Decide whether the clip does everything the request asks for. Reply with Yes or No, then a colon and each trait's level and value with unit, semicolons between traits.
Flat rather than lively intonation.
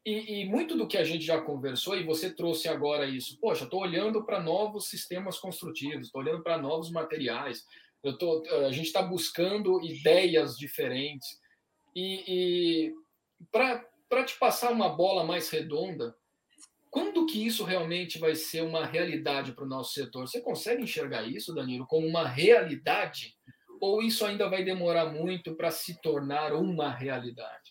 No: average, 3.8 semitones